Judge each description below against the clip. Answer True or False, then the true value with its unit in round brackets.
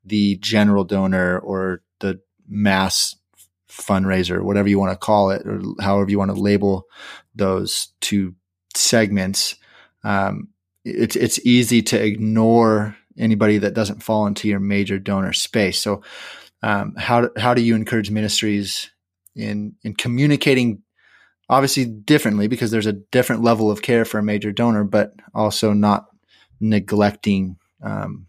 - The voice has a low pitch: True (105 Hz)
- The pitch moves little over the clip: True (2.1 semitones)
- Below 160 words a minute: True (140 wpm)